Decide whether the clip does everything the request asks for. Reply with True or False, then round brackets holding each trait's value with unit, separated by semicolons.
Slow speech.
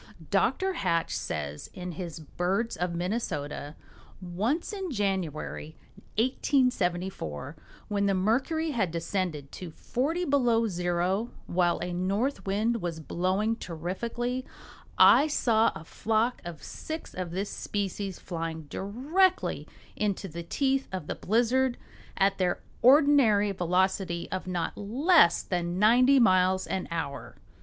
True (125 wpm)